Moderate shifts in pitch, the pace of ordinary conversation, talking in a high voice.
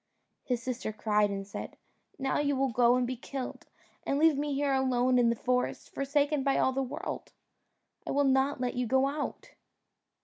No: narrow, 2.1 semitones; average, 190 wpm; very high, 260 Hz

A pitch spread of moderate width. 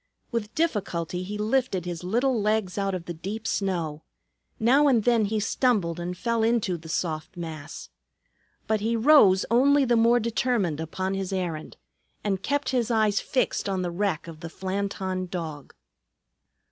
Yes: average, 4.7 semitones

